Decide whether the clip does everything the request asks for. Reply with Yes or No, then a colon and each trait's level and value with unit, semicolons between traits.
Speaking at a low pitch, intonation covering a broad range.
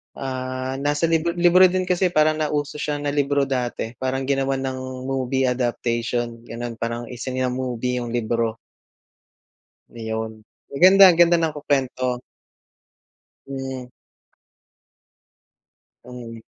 No: low, 130 Hz; average, 3.2 semitones